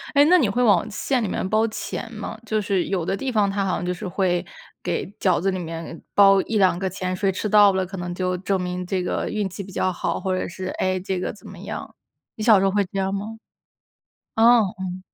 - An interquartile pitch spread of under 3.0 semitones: Yes, narrow, 2.4 semitones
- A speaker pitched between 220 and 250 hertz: No, high, 195 Hz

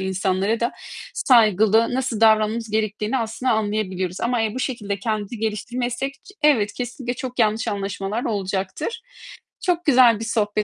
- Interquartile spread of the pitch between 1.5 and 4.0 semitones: Yes, average, 3.0 semitones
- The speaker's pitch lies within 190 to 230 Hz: Yes, high, 220 Hz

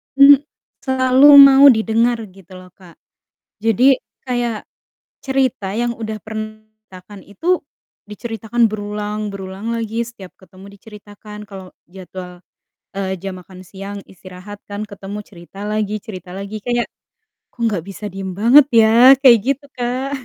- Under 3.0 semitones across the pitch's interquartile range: No, average, 3.6 semitones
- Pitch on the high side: Yes, high, 215 Hz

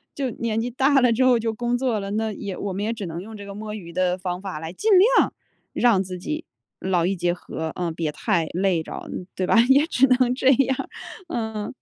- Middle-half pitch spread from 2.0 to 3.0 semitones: No, average, 5.1 semitones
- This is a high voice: Yes, high, 210 Hz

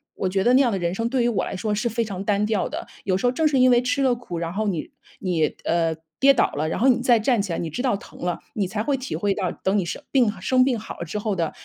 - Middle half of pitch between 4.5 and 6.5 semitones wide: Yes, average, 5.0 semitones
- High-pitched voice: Yes, high, 210 Hz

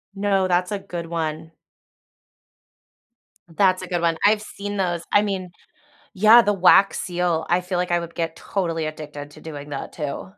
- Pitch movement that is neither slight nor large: Yes, average, 3.1 semitones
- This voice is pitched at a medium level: Yes, medium, 180 Hz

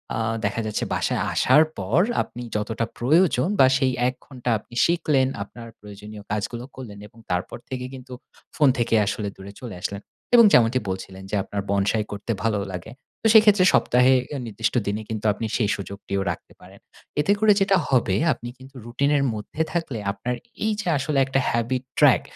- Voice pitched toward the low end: Yes, low, 120 Hz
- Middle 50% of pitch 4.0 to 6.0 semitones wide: Yes, average, 4.3 semitones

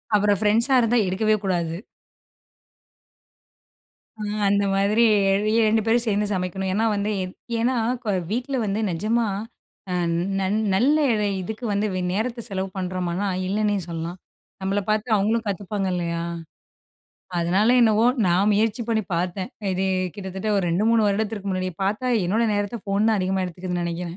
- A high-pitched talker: Yes, high, 200 Hz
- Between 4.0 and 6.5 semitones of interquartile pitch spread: No, average, 2.9 semitones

